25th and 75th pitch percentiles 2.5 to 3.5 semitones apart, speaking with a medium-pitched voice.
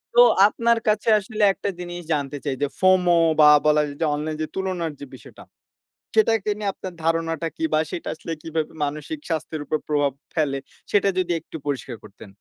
No: average, 4.0 semitones; medium, 165 Hz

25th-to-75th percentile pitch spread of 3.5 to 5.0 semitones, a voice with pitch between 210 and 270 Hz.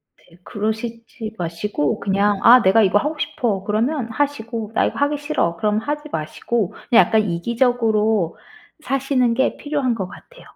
Yes: average, 4.3 semitones; high, 225 Hz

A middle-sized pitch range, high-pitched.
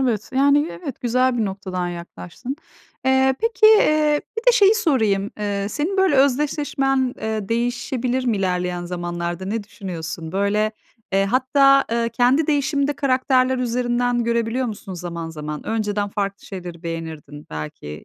No: wide, 6.3 semitones; high, 230 Hz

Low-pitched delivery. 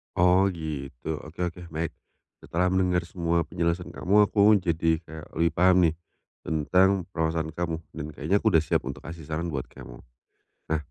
Yes: very low, 85 Hz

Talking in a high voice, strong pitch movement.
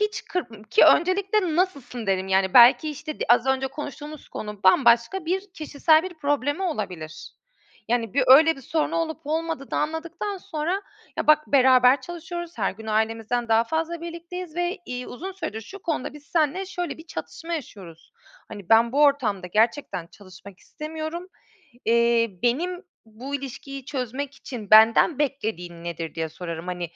Yes: very high, 275 Hz; wide, 6.6 semitones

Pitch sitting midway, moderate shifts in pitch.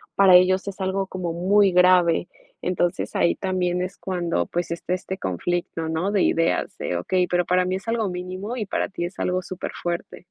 No: medium, 180 Hz; narrow, 1.4 semitones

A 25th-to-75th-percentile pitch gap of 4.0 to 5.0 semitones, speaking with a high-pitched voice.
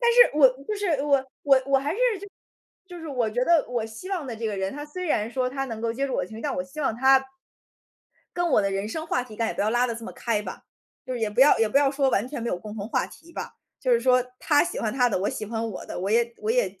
Yes: average, 4.5 semitones; very high, 255 Hz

